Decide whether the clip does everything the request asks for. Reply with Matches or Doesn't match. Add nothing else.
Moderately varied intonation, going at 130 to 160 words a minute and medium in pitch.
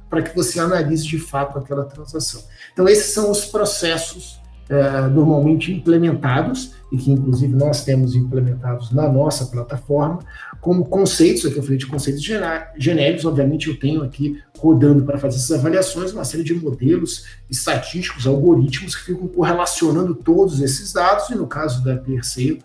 Matches